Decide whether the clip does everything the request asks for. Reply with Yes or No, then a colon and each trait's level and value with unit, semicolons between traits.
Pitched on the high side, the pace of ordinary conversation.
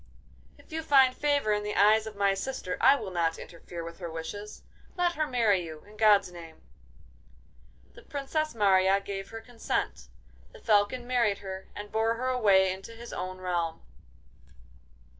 Yes: high, 205 Hz; average, 165 wpm